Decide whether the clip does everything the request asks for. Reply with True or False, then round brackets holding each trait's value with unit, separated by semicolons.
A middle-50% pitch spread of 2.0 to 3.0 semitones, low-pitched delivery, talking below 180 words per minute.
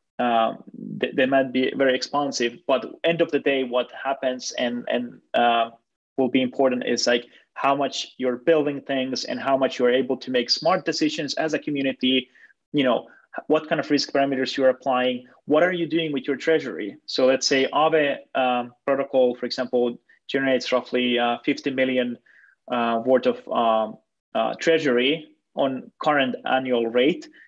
True (2.5 semitones; 130 Hz; 170 wpm)